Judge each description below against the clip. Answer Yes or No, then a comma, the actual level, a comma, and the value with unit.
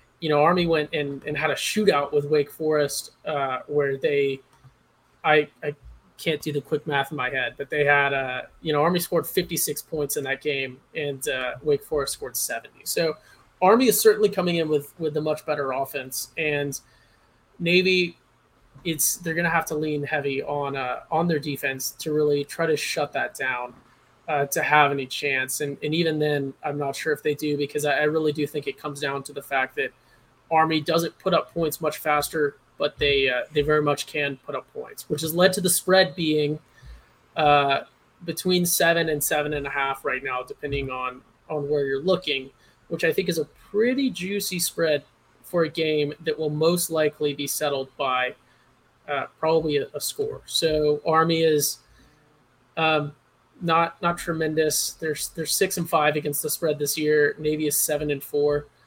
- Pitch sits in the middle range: Yes, medium, 150 Hz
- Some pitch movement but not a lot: No, narrow, 2.3 semitones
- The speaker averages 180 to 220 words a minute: Yes, average, 195 wpm